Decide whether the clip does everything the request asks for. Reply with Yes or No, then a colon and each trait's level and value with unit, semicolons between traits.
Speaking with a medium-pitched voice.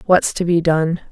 Yes: medium, 170 Hz